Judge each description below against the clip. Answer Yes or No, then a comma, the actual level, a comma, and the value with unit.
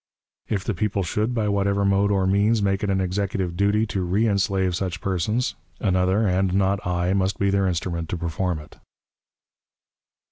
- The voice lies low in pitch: Yes, very low, 95 Hz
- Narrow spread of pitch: Yes, narrow, 1.7 semitones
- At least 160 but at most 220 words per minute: Yes, average, 170 wpm